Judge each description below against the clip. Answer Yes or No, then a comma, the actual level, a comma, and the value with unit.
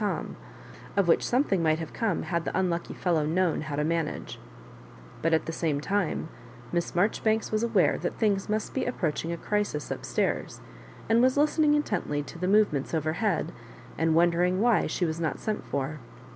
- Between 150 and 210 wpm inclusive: Yes, average, 185 wpm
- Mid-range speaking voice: Yes, medium, 175 Hz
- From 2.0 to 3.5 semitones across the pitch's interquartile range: No, average, 5.0 semitones